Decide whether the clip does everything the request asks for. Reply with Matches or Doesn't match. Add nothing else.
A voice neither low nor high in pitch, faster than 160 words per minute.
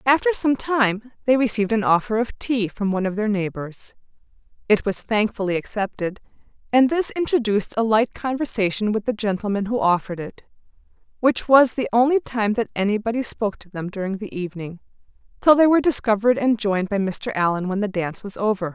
Doesn't match